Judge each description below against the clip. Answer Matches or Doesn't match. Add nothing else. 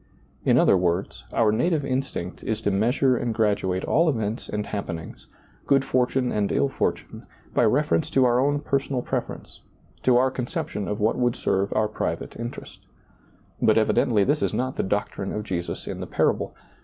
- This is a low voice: Matches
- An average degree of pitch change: Matches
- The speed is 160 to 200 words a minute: Matches